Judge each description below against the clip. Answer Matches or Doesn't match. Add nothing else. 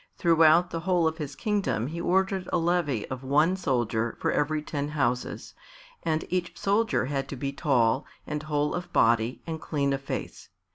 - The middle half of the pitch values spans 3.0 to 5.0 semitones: Matches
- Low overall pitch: Doesn't match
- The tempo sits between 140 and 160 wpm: Doesn't match